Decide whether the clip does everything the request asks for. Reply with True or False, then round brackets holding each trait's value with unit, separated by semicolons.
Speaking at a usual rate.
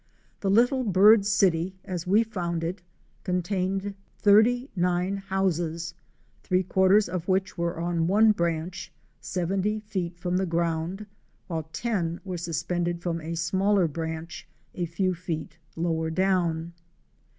False (130 wpm)